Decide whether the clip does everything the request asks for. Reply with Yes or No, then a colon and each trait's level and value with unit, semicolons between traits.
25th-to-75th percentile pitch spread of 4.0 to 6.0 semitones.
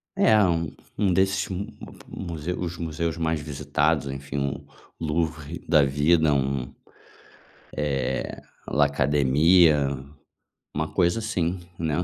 No: average, 3.2 semitones